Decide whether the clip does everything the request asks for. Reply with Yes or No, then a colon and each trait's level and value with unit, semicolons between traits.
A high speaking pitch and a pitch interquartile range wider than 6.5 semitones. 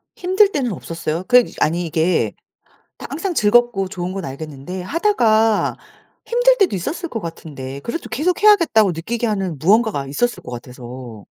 Yes: high, 195 Hz; wide, 8.5 semitones